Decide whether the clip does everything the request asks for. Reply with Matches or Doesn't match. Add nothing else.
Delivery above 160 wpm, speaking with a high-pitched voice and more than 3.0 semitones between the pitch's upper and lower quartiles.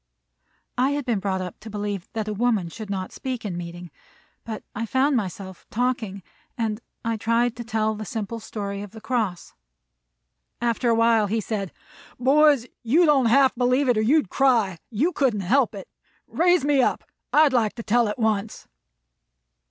Matches